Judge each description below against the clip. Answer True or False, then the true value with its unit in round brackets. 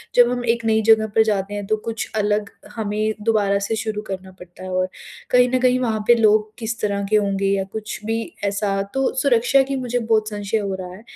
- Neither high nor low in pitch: False (215 Hz)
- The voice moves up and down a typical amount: False (2.3 semitones)